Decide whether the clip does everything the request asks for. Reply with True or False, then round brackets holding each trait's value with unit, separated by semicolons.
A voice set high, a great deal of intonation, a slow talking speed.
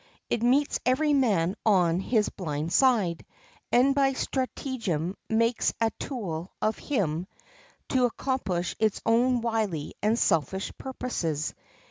True (220 Hz; 6.5 semitones; 120 wpm)